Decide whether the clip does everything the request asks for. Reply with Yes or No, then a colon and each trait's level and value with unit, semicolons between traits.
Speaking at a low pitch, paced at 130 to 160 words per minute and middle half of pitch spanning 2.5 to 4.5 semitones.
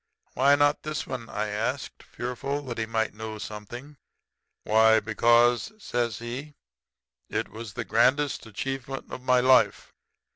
Yes: low, 120 Hz; average, 140 wpm; average, 3.3 semitones